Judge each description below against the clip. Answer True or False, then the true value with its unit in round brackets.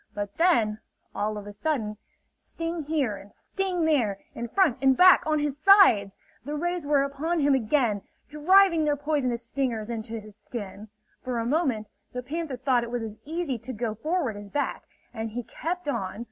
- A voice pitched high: True (260 Hz)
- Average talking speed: True (185 wpm)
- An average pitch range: False (6.1 semitones)